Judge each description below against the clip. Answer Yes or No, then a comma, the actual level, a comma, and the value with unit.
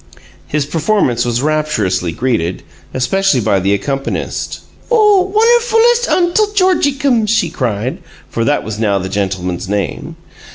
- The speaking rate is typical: No, slow, 125 wpm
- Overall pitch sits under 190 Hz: Yes, medium, 140 Hz